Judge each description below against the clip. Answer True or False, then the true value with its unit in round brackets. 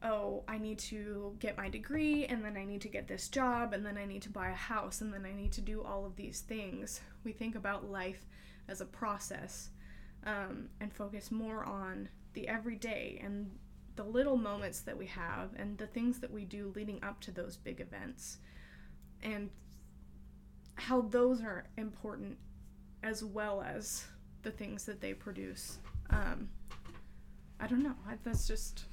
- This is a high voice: True (210 Hz)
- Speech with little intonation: True (2.3 semitones)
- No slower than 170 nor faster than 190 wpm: True (175 wpm)